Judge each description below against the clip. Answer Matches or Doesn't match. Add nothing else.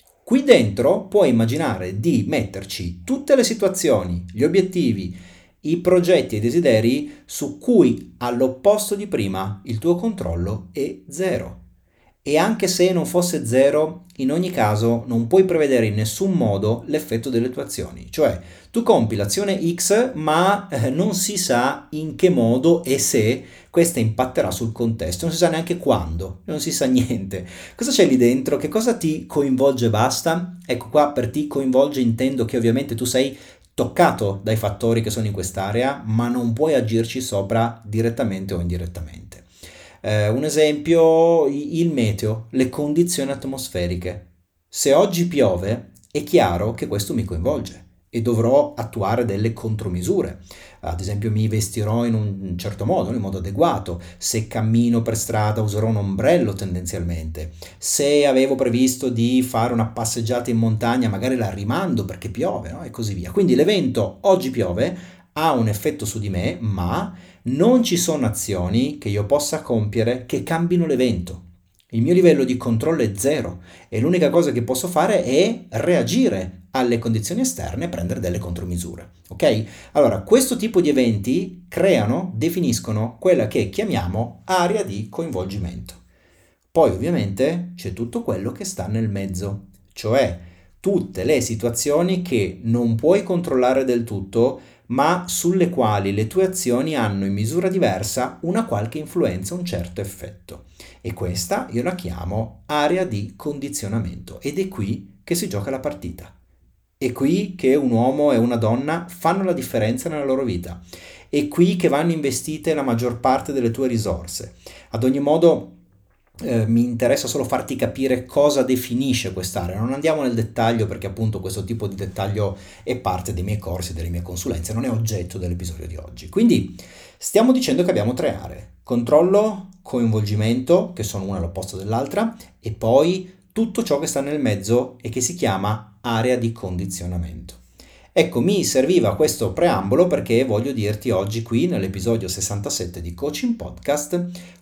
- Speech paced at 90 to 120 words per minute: Doesn't match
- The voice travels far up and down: Matches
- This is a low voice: Matches